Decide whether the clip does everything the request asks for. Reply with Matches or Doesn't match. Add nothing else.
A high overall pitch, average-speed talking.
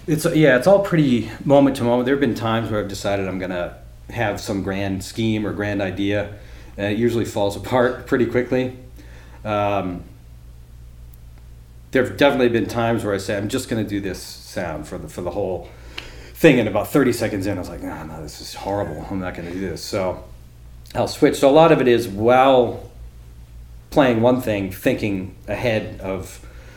Doesn't match